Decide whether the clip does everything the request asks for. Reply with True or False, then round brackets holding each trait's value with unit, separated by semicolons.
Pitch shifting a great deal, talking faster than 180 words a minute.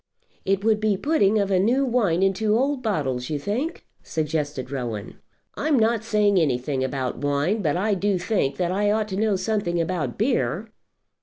False (6.3 semitones; 175 wpm)